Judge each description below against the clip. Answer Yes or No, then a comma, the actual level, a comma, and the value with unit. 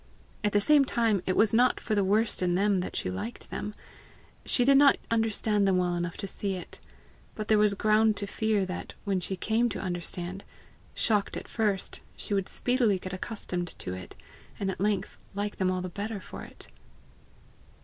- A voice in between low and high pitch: No, high, 200 Hz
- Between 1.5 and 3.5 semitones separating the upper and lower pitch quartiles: Yes, average, 2.9 semitones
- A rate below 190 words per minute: No, average, 195 wpm